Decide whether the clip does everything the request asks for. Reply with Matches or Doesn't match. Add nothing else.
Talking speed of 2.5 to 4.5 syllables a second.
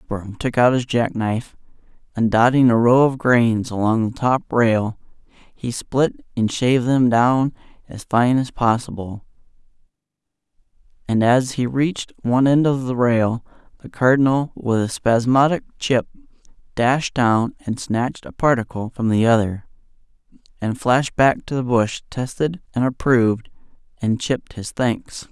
Matches